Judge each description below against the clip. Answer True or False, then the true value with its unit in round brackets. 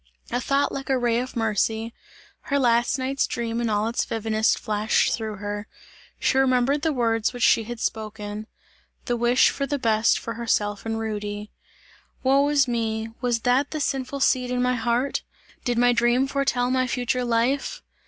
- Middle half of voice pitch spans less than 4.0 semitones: True (2.6 semitones)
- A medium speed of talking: True (175 wpm)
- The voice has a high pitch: True (240 Hz)